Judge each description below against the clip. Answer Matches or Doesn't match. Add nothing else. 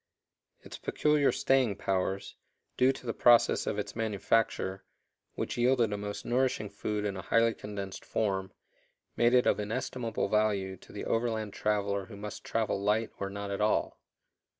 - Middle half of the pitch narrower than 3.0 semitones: Matches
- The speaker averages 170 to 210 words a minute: Doesn't match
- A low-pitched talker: Matches